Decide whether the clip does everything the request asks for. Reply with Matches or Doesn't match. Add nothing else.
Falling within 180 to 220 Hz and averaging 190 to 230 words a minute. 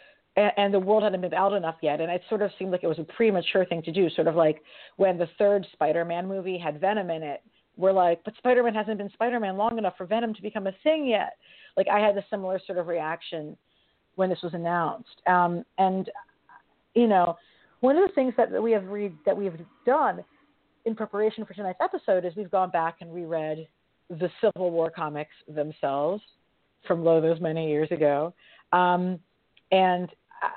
Matches